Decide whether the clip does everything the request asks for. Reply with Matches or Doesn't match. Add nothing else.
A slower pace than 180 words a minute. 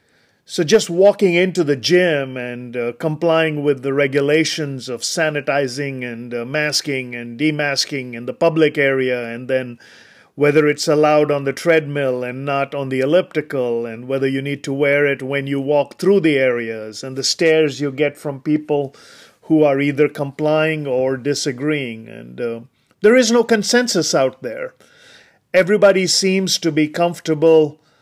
Matches